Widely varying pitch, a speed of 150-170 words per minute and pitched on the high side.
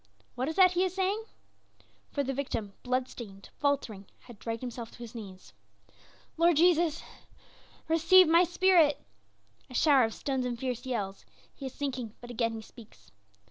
Yes: wide, 6.1 semitones; average, 165 wpm; very high, 260 Hz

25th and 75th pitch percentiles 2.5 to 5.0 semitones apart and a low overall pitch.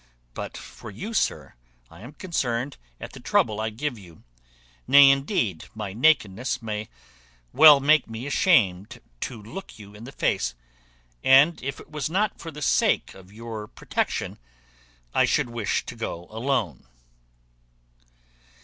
No: wide, 5.4 semitones; low, 120 Hz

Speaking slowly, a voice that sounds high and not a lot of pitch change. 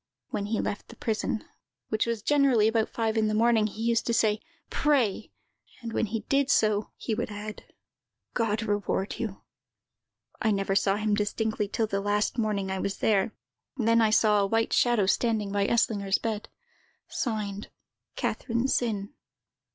No: average, 165 wpm; high, 215 Hz; narrow, 1.9 semitones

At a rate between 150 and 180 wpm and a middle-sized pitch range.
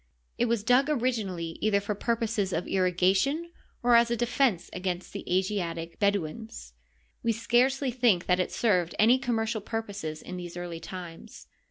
Yes: average, 155 wpm; average, 4.8 semitones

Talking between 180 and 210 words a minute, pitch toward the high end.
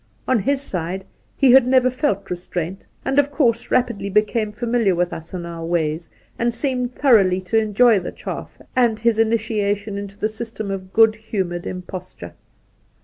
No: average, 165 wpm; high, 215 Hz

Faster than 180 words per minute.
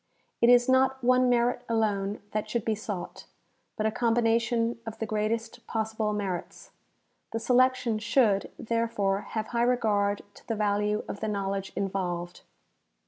No: average, 145 wpm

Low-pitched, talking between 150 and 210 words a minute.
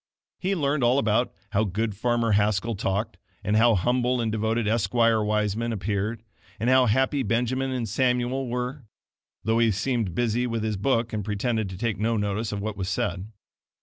Yes: low, 115 Hz; average, 180 wpm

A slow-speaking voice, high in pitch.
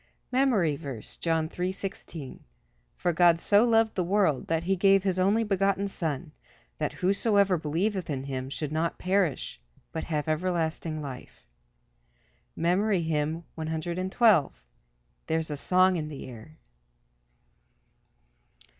No: slow, 120 wpm; medium, 170 Hz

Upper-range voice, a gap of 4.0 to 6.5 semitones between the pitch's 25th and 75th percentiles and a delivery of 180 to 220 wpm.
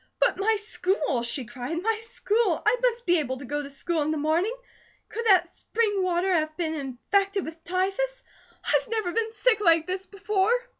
Yes: very high, 370 Hz; wide, 5.5 semitones; average, 190 wpm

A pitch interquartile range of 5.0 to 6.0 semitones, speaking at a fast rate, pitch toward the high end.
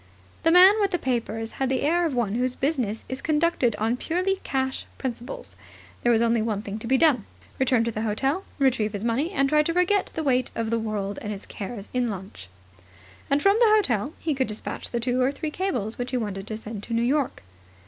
Yes: average, 5.3 semitones; fast, 225 wpm; very high, 250 Hz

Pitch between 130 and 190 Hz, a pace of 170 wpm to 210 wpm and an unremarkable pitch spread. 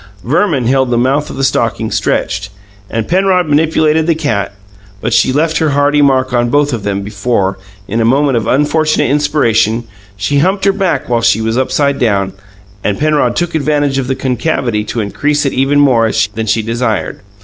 Yes: low, 135 Hz; average, 185 wpm; average, 4.5 semitones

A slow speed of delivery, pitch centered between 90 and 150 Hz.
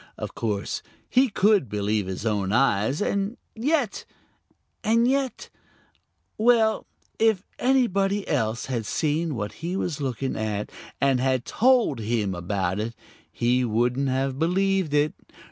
Yes: slow, 130 wpm; low, 135 Hz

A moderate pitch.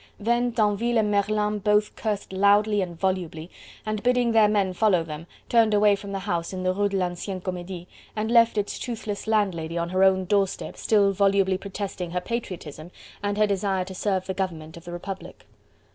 No: high, 200 Hz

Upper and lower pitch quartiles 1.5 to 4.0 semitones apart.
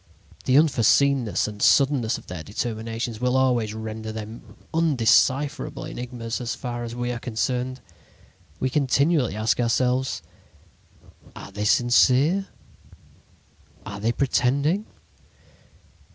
Yes: average, 3.1 semitones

